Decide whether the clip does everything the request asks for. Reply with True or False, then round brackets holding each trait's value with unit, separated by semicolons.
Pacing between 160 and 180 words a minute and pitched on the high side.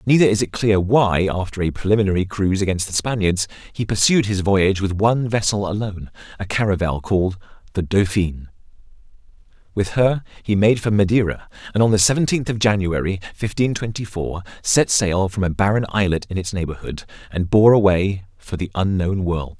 False (170 wpm; 100 Hz)